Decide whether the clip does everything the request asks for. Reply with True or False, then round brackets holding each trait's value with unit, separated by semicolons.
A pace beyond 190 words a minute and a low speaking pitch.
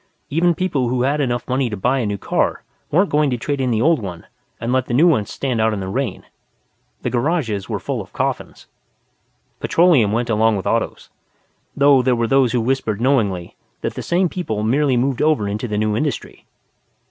True (205 wpm; 125 Hz)